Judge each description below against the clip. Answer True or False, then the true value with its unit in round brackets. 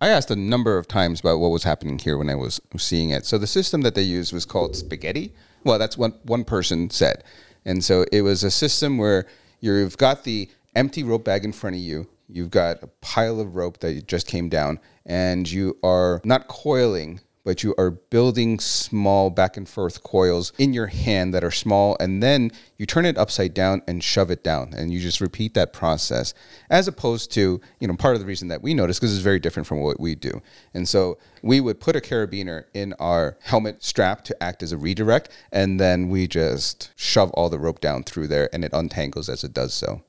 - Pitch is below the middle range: True (95 Hz)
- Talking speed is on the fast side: True (225 wpm)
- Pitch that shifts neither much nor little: True (4.0 semitones)